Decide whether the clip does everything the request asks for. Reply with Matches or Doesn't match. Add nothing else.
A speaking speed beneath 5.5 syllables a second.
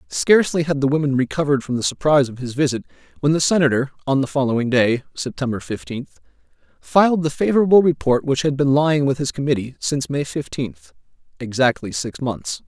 Doesn't match